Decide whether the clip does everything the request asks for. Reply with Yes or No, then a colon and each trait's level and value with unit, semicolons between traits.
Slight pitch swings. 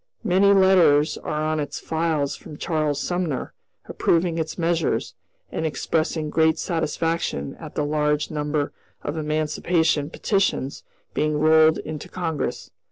Yes: narrow, 1.9 semitones